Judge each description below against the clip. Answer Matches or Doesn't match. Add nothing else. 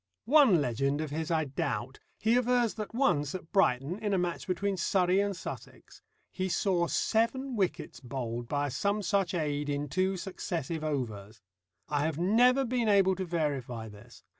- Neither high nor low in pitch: Matches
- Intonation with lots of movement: Matches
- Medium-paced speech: Matches